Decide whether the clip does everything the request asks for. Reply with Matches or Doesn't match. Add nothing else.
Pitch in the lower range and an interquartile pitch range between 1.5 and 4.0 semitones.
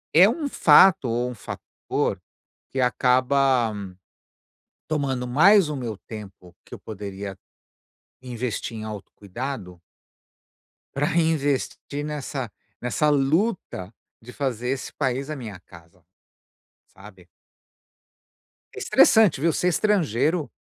Doesn't match